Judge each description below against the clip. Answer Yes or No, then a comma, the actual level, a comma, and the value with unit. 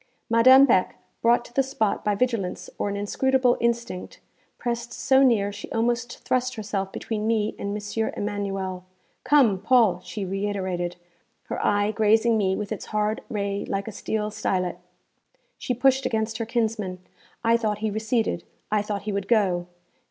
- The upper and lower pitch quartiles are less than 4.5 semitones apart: Yes, average, 2.9 semitones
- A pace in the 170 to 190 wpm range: No, average, 160 wpm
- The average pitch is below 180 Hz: No, high, 215 Hz